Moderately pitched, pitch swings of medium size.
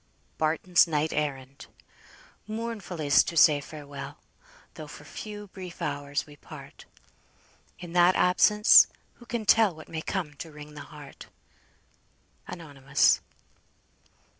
Yes: medium, 155 Hz; average, 3.9 semitones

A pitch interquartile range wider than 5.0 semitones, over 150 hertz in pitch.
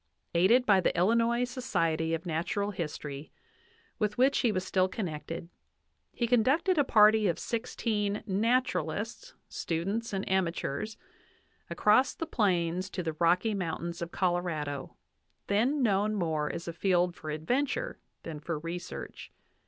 Yes: wide, 5.4 semitones; high, 190 Hz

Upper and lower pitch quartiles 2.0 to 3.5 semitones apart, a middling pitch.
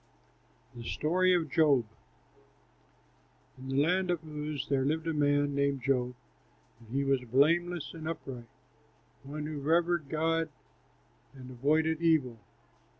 Yes: average, 3.1 semitones; medium, 150 Hz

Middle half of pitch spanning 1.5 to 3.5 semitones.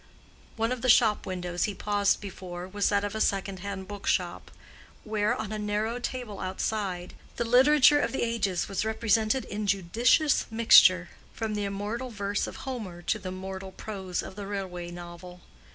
Yes: average, 2.9 semitones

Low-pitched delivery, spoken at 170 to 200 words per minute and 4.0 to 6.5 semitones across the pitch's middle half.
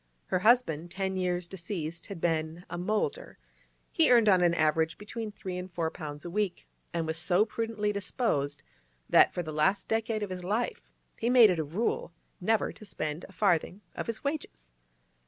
No: medium, 185 Hz; average, 175 wpm; average, 4.6 semitones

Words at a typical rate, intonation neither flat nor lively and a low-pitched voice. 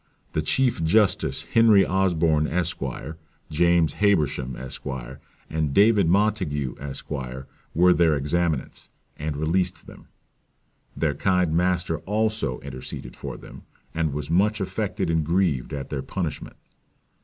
No: slow, 120 wpm; average, 4.4 semitones; very low, 80 Hz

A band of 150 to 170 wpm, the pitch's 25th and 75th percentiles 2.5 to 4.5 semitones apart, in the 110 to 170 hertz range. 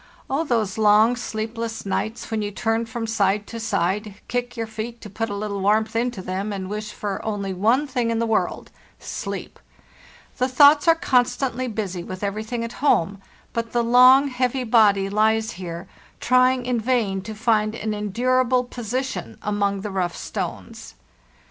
No: average, 165 wpm; average, 3.1 semitones; high, 220 Hz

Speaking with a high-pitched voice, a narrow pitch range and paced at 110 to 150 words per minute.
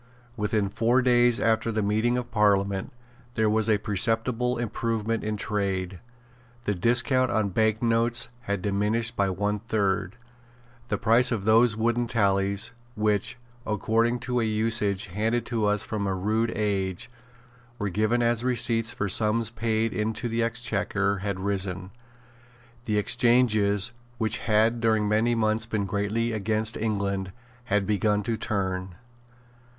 No: low, 110 Hz; narrow, 2.3 semitones; average, 140 wpm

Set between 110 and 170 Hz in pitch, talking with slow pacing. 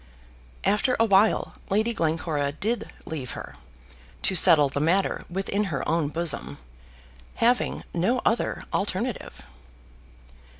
No: high, 190 Hz; slow, 115 wpm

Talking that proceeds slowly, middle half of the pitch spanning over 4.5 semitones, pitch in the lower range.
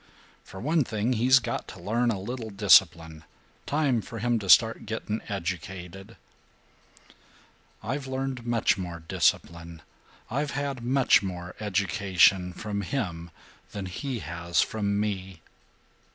Yes: slow, 125 wpm; average, 5.0 semitones; low, 105 Hz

